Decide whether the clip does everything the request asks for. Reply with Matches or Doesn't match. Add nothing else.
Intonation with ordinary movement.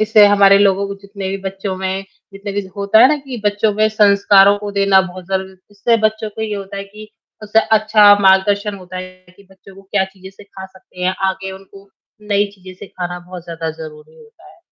Doesn't match